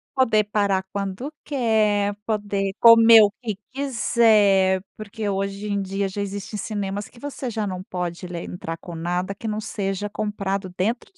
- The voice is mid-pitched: No, high, 205 Hz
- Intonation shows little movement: Yes, narrow, 2.2 semitones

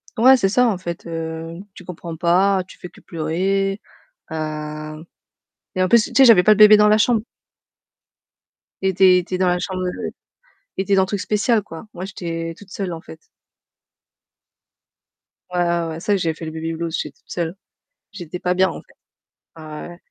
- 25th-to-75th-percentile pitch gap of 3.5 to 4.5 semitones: No, average, 3.0 semitones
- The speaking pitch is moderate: Yes, medium, 180 Hz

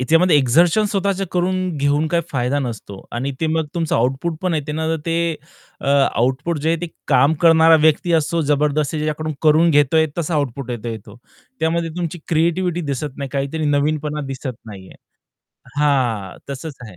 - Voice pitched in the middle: Yes, medium, 150 Hz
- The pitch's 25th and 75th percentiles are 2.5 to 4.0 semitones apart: Yes, average, 3.3 semitones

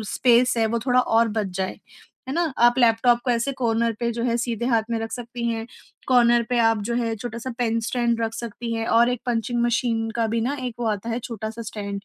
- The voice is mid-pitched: No, high, 235 Hz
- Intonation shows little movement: Yes, narrow, 1.2 semitones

